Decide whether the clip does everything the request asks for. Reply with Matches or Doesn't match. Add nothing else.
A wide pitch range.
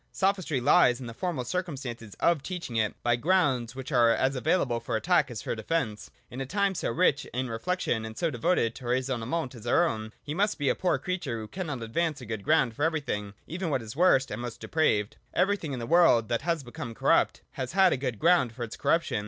Matches